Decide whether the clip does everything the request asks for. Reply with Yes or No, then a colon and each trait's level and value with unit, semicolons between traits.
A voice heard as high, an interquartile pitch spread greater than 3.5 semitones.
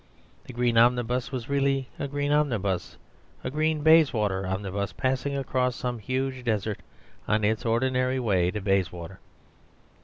No: low, 120 Hz; average, 4.6 semitones